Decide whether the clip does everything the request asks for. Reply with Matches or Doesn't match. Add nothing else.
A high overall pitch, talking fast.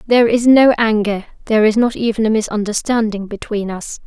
Doesn't match